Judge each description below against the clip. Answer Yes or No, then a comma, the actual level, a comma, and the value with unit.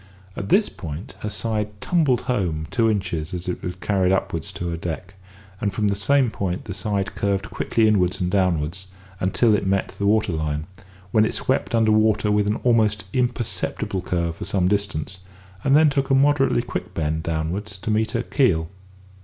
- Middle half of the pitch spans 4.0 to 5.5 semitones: No, average, 3.6 semitones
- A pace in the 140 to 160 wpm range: No, average, 185 wpm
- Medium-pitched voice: No, low, 100 Hz